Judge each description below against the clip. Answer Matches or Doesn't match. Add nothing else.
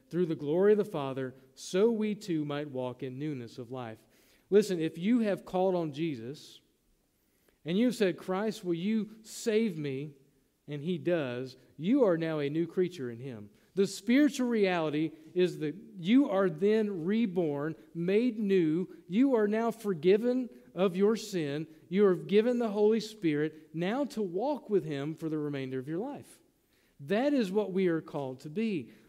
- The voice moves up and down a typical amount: Doesn't match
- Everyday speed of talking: Matches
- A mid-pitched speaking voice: Matches